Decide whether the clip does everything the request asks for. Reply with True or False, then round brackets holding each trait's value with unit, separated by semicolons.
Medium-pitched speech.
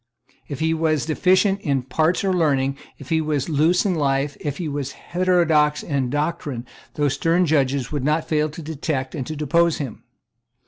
True (150 Hz)